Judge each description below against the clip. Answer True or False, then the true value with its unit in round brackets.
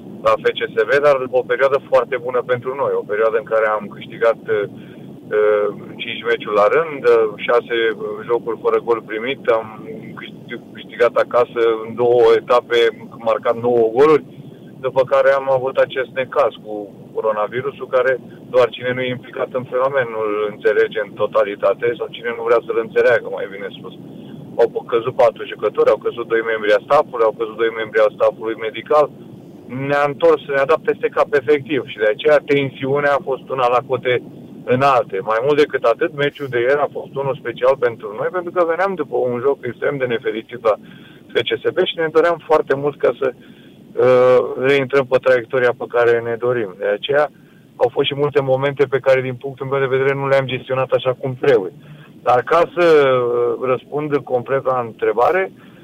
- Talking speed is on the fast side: True (175 wpm)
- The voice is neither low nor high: True (165 Hz)